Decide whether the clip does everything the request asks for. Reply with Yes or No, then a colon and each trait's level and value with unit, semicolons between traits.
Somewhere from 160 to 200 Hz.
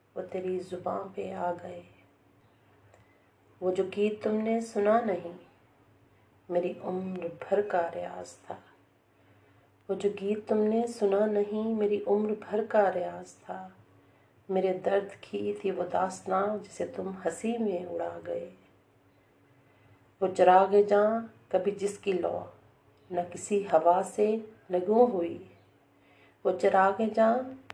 Yes: medium, 185 Hz